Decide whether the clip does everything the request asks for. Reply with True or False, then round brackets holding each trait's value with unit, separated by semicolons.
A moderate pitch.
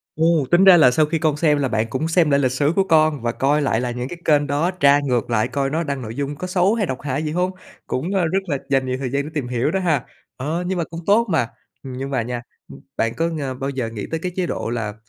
True (145 Hz)